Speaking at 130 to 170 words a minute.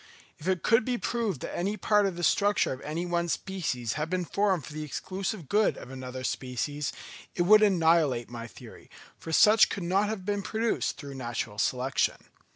No: average, 190 wpm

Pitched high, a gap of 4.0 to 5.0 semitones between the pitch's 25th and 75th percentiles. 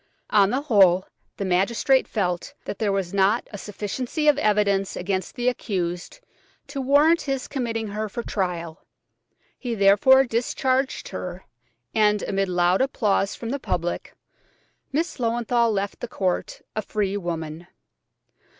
Yes: high, 210 Hz; average, 4.6 semitones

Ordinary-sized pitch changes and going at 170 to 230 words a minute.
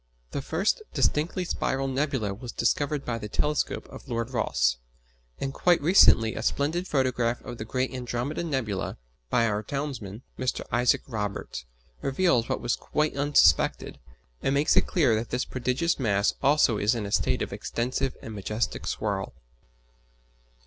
No: average, 4.2 semitones; average, 155 wpm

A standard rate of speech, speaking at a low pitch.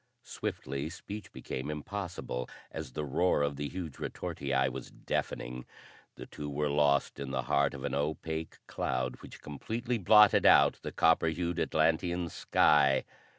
Yes: average, 150 wpm; very low, 75 Hz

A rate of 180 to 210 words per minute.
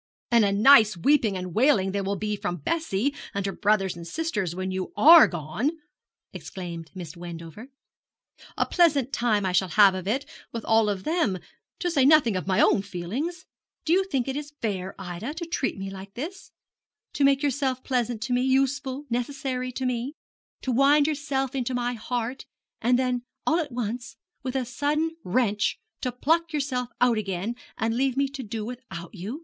Yes: average, 185 wpm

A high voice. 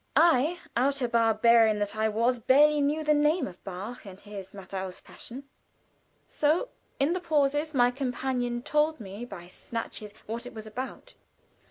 Yes: high, 245 Hz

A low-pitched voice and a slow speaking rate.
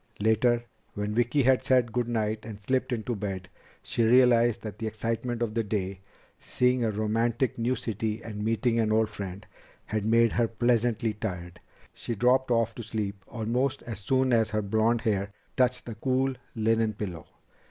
No: low, 115 Hz; average, 175 wpm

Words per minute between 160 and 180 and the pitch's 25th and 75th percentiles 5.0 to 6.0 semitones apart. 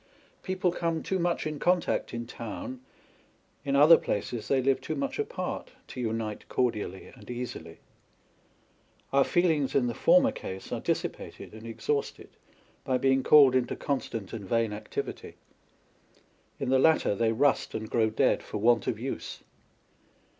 No: average, 150 wpm; wide, 5.4 semitones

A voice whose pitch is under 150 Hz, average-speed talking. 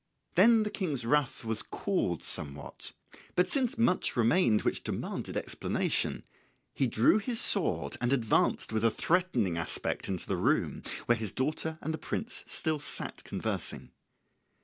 Yes: medium, 140 Hz; average, 150 wpm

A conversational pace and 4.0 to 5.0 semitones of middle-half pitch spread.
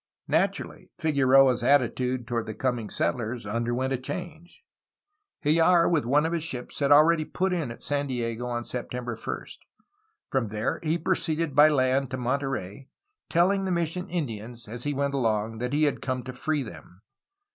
Yes: average, 170 wpm; average, 4.4 semitones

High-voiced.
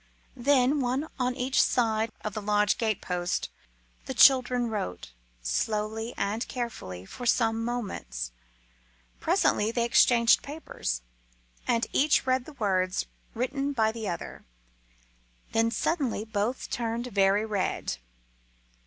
Yes: high, 225 Hz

